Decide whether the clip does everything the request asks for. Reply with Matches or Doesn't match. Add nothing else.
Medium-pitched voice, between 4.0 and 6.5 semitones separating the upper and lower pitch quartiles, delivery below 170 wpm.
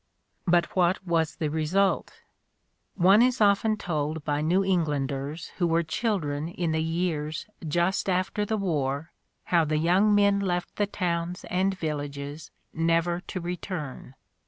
Doesn't match